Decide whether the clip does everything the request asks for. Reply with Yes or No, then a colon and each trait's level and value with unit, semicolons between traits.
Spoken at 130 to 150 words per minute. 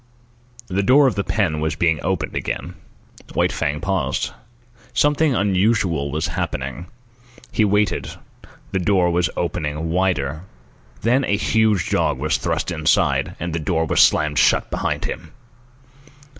Yes: average, 140 wpm